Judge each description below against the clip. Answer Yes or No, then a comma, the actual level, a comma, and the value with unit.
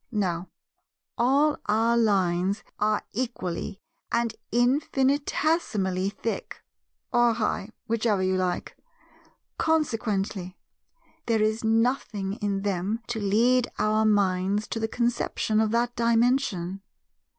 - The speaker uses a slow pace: Yes, slow, 105 wpm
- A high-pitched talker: Yes, high, 220 Hz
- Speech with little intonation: No, average, 3.4 semitones